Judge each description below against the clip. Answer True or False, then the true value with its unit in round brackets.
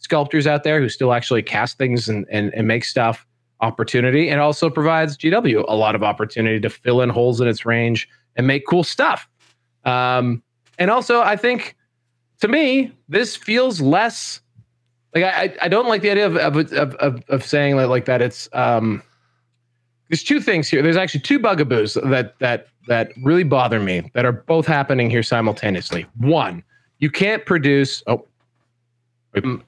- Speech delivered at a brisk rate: False (175 wpm)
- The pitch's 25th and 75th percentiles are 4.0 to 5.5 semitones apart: True (4.7 semitones)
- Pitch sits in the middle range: False (125 Hz)